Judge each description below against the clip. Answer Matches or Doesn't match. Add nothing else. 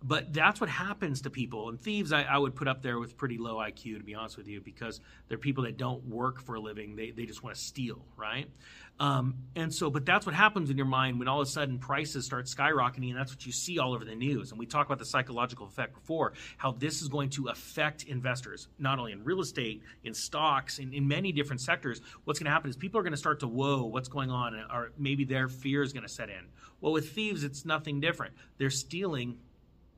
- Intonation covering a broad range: Doesn't match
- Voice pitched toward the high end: Doesn't match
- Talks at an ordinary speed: Doesn't match